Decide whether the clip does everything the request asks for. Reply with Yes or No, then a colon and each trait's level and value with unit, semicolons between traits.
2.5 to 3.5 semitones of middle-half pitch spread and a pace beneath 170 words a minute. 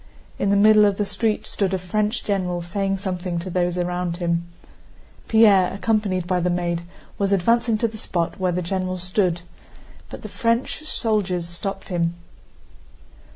Yes: average, 2.9 semitones; average, 160 wpm